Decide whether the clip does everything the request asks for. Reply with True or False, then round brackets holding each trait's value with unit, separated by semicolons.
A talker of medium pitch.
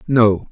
False (110 Hz)